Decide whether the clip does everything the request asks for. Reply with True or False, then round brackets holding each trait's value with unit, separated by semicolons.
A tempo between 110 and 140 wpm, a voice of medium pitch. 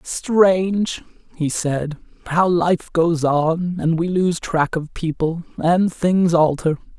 True (135 wpm; 170 Hz)